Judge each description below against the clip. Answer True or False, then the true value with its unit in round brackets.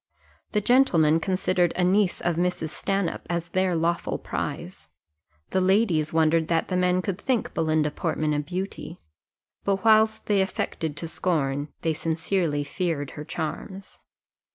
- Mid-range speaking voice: True (175 Hz)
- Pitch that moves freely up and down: False (3.3 semitones)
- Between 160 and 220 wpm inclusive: False (145 wpm)